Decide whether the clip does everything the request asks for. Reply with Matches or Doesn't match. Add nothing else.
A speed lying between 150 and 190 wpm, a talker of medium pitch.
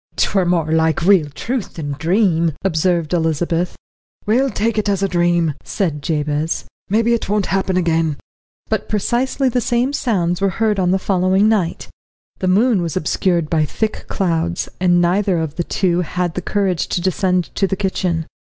Matches